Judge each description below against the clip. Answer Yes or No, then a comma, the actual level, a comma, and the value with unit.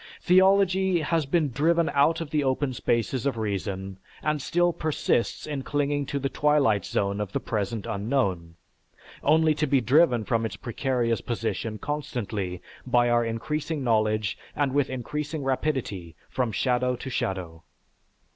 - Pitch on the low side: Yes, low, 130 Hz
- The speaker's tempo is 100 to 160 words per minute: Yes, average, 145 wpm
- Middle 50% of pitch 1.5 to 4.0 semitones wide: No, wide, 5.4 semitones